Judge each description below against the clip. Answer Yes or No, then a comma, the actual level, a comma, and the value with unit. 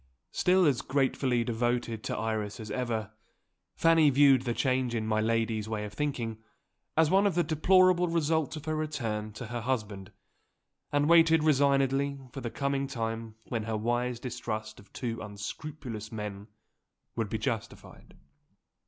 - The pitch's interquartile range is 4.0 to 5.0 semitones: Yes, average, 4.7 semitones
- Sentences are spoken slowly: No, average, 155 wpm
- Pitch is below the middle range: Yes, low, 120 Hz